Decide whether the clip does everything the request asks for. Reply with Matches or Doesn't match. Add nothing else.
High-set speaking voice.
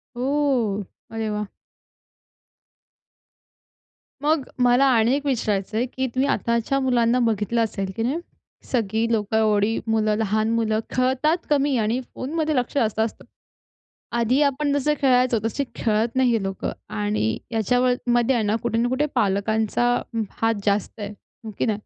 Matches